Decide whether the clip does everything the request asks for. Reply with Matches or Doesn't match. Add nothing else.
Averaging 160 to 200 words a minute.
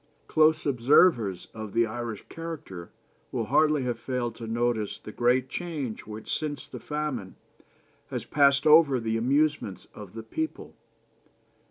Doesn't match